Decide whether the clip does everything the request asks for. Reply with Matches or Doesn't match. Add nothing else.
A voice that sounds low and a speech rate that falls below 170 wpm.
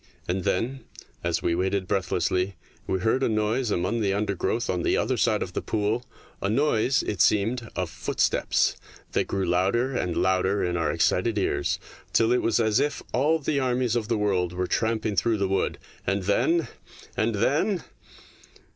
Doesn't match